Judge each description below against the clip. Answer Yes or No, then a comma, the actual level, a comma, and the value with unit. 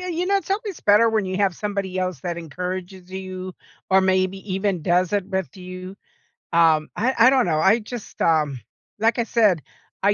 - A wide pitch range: No, average, 2.8 semitones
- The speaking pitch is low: No, high, 190 Hz